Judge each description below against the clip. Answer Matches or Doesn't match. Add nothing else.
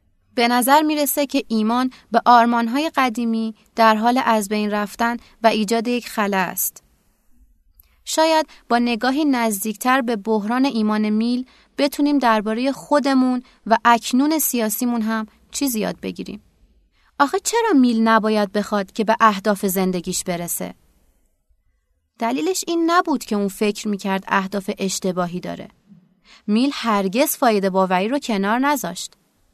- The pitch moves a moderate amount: Matches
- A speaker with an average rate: Matches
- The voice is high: Matches